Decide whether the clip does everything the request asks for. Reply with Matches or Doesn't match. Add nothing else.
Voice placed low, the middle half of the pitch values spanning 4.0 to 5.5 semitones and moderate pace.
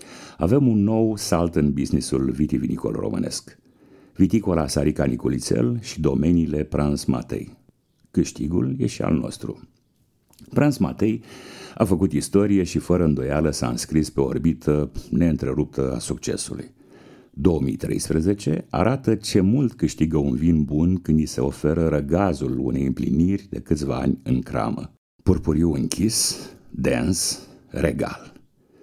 Matches